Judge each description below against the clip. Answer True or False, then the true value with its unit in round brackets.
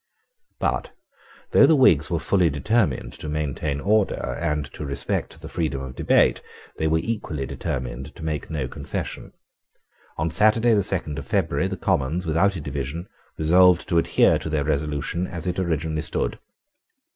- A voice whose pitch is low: True (80 Hz)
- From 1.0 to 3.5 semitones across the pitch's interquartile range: False (4.0 semitones)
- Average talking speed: True (160 wpm)